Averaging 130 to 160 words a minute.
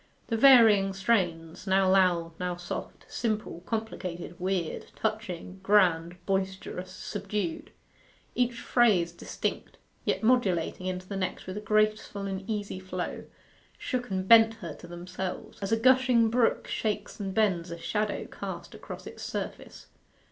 Yes: average, 140 wpm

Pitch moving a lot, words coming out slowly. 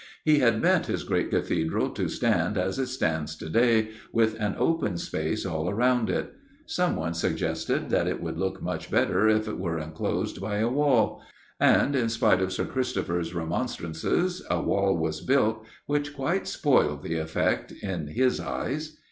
No: wide, 7.4 semitones; average, 170 wpm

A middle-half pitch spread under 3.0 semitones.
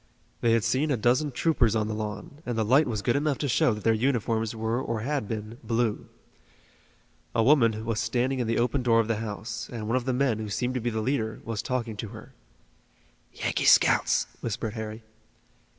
Yes: narrow, 2.5 semitones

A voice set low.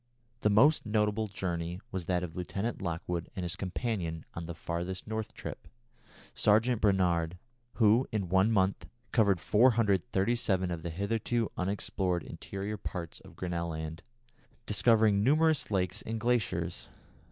Yes: very low, 95 Hz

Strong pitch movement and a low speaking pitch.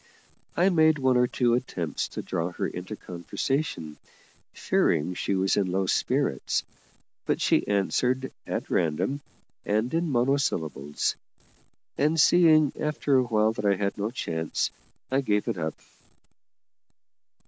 Yes: wide, 7.1 semitones; low, 110 Hz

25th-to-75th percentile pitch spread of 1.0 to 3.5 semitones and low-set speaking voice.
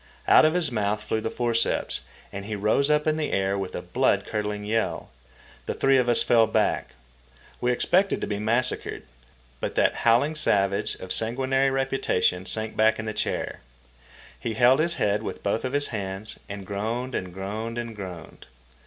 No: average, 4.1 semitones; low, 110 Hz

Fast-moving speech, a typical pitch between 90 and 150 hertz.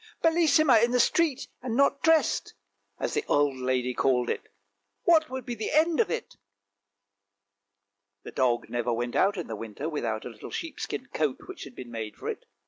Yes: fast, 210 wpm; medium, 140 Hz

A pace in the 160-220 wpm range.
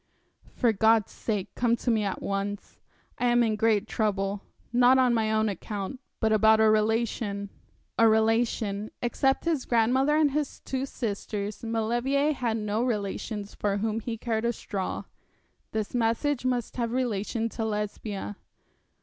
No: average, 150 wpm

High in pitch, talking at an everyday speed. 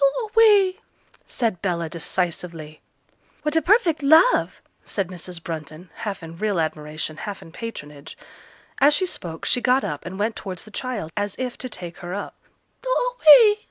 Yes: high, 205 Hz; average, 165 wpm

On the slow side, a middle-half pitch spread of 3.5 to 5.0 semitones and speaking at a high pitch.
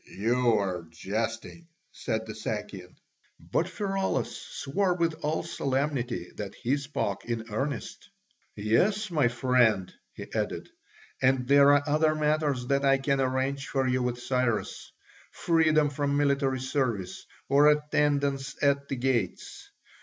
No: slow, 130 wpm; average, 3.9 semitones; low, 135 Hz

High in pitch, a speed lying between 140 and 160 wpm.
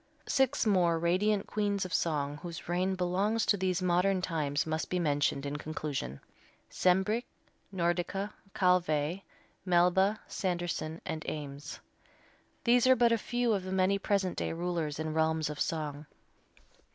No: medium, 180 Hz; average, 145 wpm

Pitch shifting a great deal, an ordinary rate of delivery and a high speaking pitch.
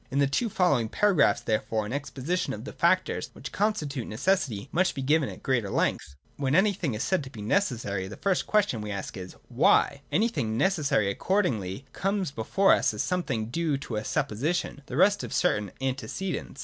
No: wide, 8.8 semitones; average, 190 wpm; medium, 140 Hz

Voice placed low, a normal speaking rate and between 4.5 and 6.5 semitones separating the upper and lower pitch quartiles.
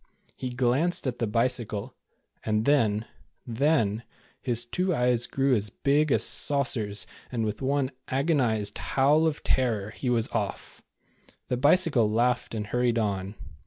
No: low, 125 Hz; average, 150 wpm; average, 4.1 semitones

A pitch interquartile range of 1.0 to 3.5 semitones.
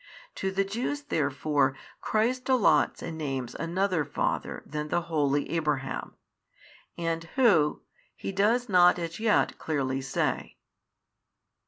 No: average, 5.3 semitones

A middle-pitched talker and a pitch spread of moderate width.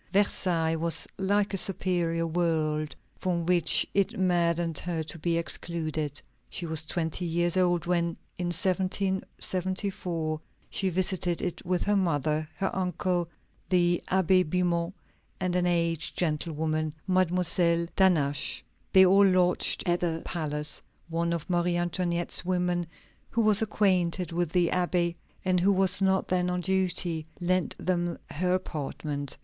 No: medium, 175 Hz; narrow, 1.8 semitones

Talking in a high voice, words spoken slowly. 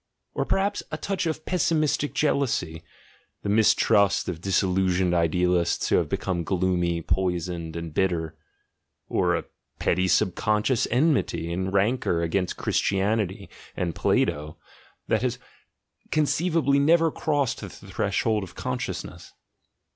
No: very low, 95 Hz; slow, 115 wpm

